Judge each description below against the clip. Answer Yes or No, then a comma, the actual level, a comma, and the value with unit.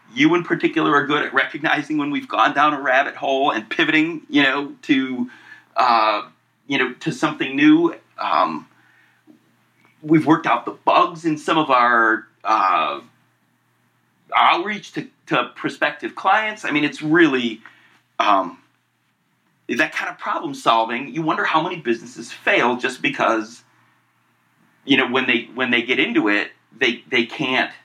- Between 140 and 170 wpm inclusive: Yes, average, 155 wpm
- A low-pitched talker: No, very high, 270 Hz